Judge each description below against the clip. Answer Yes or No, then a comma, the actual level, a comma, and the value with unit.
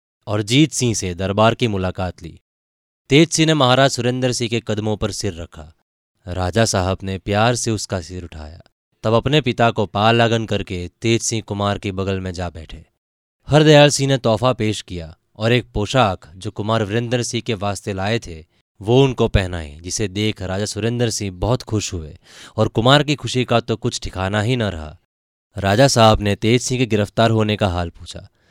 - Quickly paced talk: Yes, fast, 195 wpm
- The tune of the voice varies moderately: Yes, average, 4.1 semitones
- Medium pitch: No, low, 105 Hz